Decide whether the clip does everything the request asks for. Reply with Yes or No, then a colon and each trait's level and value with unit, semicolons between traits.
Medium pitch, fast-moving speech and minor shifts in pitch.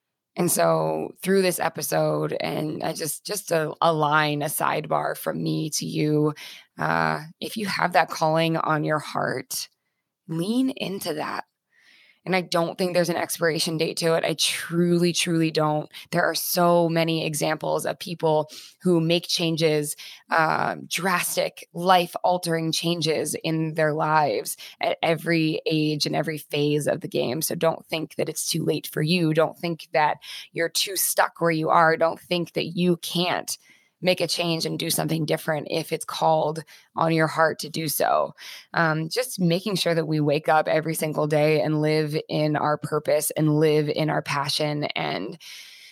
No: medium, 160 Hz; average, 170 wpm; narrow, 2.0 semitones